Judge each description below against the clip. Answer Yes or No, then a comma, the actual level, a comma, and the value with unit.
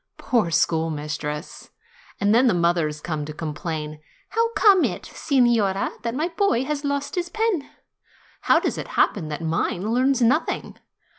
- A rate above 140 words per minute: Yes, average, 155 wpm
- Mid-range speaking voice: No, high, 215 Hz